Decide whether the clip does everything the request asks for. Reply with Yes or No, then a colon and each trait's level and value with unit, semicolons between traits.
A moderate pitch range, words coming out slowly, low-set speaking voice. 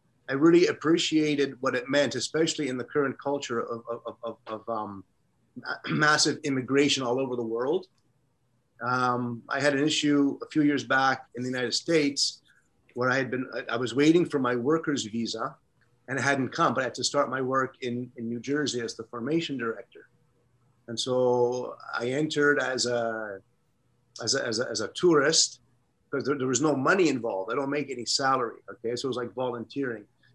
No: average, 3.1 semitones; average, 190 wpm; low, 130 Hz